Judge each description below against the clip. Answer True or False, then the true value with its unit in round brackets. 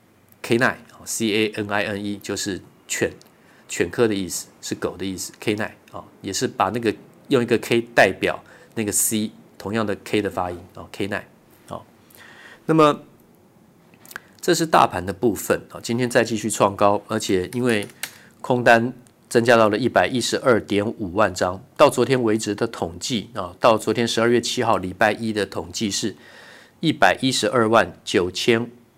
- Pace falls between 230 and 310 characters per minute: True (250 characters per minute)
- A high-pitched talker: False (110 Hz)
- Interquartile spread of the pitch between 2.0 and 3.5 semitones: True (2.8 semitones)